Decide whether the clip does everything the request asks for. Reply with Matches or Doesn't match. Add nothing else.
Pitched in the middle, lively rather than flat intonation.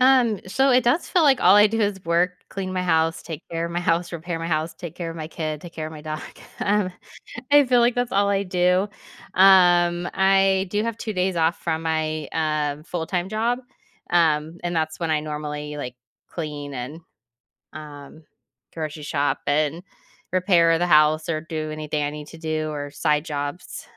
Doesn't match